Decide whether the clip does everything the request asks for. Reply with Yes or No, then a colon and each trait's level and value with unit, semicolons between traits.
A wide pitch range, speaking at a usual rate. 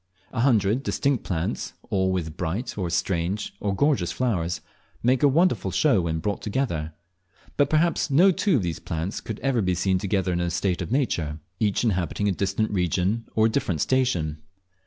Yes: wide, 6.4 semitones; average, 180 wpm